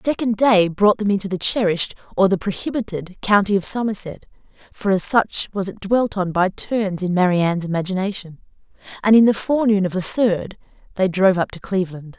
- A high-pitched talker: Yes, high, 195 Hz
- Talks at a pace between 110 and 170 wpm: No, average, 185 wpm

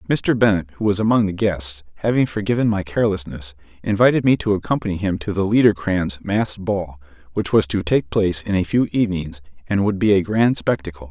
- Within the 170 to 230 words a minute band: Yes, average, 195 wpm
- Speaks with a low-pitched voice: Yes, very low, 95 Hz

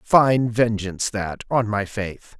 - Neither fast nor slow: Yes, average, 150 wpm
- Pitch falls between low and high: No, low, 110 Hz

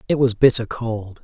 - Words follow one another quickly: No, average, 195 wpm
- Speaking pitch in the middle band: No, low, 115 Hz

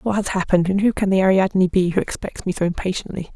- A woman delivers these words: Yes, female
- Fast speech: Yes, fast, 250 wpm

